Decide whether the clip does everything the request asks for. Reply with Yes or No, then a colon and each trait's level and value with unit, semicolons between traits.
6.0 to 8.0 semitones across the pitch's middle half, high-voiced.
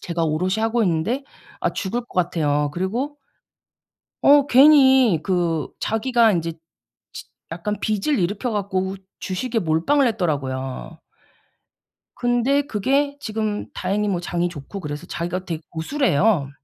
Yes: wide, 6.4 semitones; high, 195 Hz